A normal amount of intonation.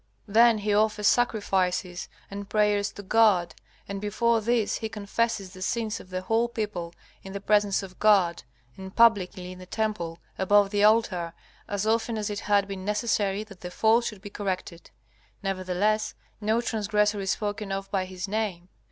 No: narrow, 2.3 semitones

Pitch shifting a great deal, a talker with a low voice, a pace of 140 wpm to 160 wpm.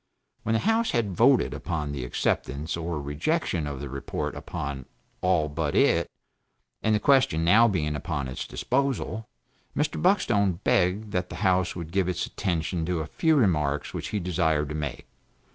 No: wide, 6.3 semitones; very low, 90 Hz; average, 170 wpm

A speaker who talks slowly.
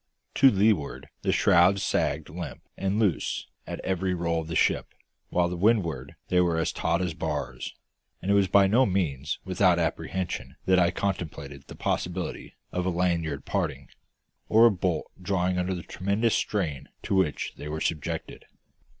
No: average, 165 wpm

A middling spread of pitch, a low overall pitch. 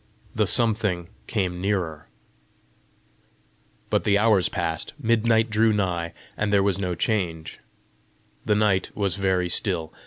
Yes: average, 3.4 semitones; low, 100 Hz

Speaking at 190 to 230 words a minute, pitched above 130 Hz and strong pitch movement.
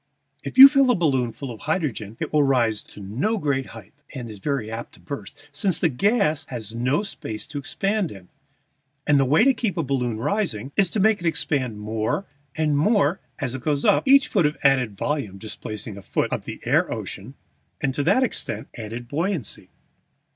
Yes: average, 200 wpm; medium, 140 Hz; wide, 7.3 semitones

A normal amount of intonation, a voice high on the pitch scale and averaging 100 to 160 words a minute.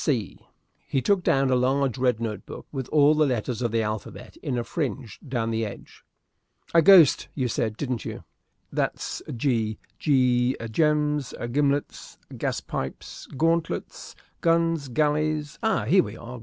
No: average, 4.4 semitones; low, 135 Hz; average, 150 wpm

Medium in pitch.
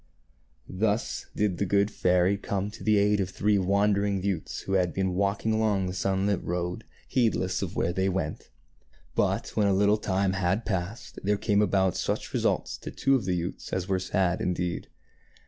No: very low, 95 Hz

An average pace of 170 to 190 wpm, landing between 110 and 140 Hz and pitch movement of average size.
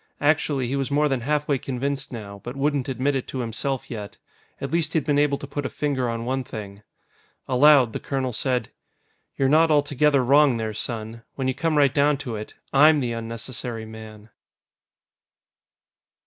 Yes: average, 175 wpm; low, 135 Hz; average, 3.8 semitones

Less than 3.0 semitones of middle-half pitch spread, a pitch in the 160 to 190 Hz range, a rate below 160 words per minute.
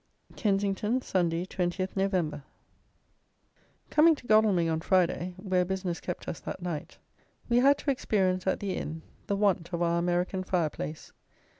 Yes: narrow, 2.6 semitones; medium, 185 Hz; average, 150 wpm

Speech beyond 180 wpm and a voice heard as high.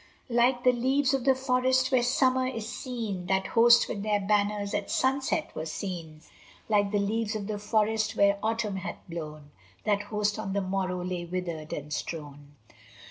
No: average, 175 wpm; high, 210 Hz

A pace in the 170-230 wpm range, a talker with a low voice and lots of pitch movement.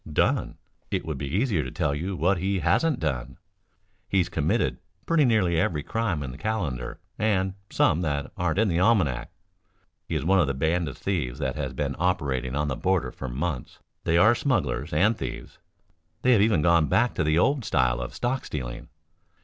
Yes: average, 190 wpm; very low, 80 Hz; wide, 5.9 semitones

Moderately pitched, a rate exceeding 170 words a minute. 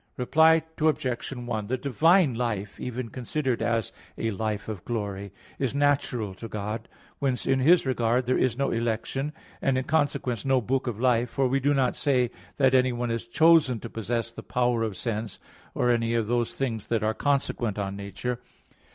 No: low, 120 Hz; average, 180 wpm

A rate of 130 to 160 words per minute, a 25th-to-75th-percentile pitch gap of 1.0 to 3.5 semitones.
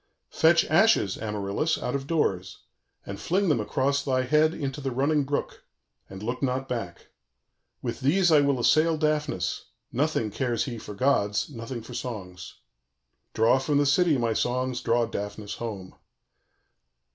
No: average, 155 wpm; average, 5.2 semitones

